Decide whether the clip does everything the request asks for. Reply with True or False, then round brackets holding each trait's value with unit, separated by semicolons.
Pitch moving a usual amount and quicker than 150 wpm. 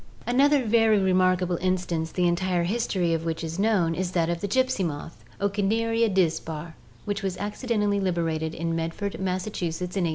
True (3.5 semitones; 170 wpm)